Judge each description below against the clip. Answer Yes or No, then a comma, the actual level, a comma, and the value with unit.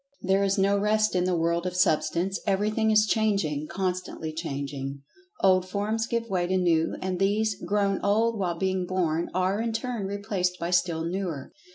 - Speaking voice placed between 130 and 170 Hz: No, medium, 185 Hz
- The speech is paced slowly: No, average, 170 wpm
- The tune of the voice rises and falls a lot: No, average, 2.9 semitones